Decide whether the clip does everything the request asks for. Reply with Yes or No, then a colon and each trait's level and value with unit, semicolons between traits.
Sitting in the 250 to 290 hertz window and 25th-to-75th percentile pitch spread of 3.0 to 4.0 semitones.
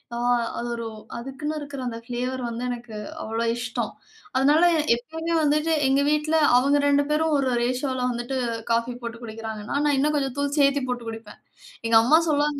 Yes: very high, 265 Hz; average, 3.5 semitones